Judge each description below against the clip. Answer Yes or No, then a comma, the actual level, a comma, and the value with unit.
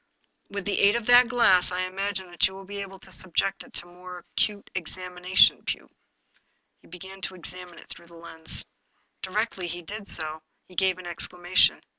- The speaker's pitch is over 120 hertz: Yes, medium, 185 Hz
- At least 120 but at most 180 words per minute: No, average, 195 wpm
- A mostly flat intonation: Yes, narrow, 1.8 semitones